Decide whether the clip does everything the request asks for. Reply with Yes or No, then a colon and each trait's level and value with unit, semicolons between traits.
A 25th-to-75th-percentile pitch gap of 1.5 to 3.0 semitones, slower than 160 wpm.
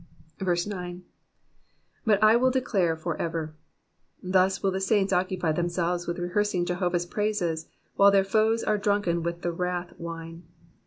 Yes: average, 2.7 semitones; average, 145 wpm